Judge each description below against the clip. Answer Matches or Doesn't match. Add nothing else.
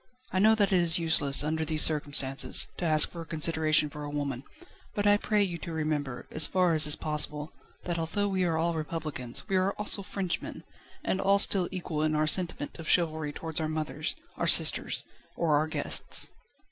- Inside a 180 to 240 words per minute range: Matches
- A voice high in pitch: Doesn't match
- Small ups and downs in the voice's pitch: Doesn't match